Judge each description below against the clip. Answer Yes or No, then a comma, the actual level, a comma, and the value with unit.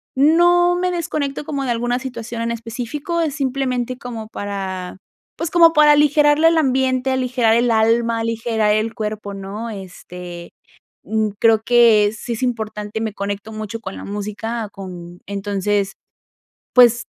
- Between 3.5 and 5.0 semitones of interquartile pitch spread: Yes, average, 4.0 semitones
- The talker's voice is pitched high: Yes, high, 230 Hz